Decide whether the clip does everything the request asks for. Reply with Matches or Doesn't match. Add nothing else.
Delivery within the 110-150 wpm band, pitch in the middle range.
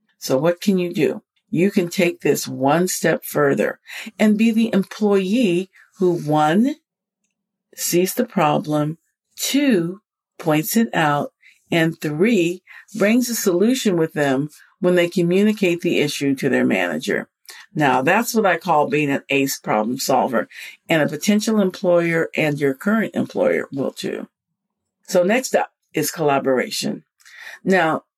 Matches